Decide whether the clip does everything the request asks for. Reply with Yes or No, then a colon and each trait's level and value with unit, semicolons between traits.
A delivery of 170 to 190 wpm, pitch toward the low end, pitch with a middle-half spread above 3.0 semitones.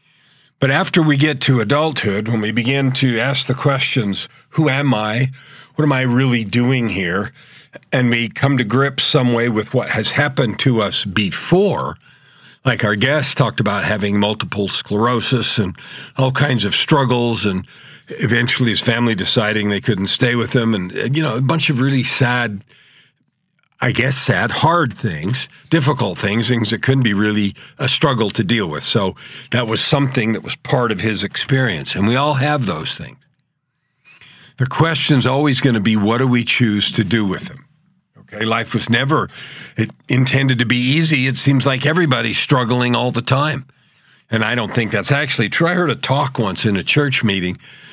Yes: average, 185 wpm; low, 130 Hz; average, 3.9 semitones